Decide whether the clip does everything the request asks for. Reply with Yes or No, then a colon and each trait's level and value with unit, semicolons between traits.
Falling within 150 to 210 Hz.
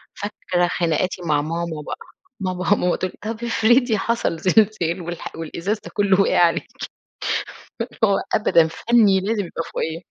Yes: medium, 185 Hz